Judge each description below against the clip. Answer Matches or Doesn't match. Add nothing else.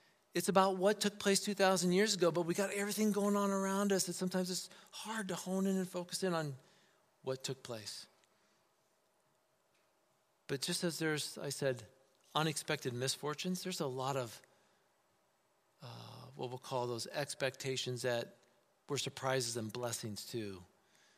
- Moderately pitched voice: Matches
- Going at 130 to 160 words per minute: Matches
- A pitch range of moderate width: Doesn't match